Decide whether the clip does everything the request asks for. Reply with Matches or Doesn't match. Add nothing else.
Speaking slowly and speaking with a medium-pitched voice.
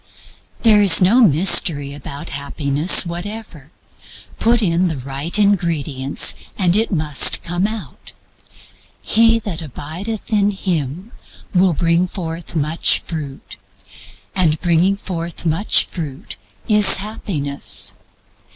Matches